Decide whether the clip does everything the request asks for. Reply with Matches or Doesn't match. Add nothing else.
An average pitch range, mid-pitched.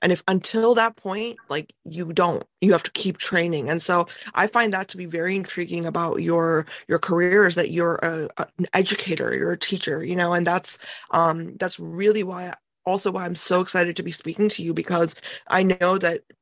Doesn't match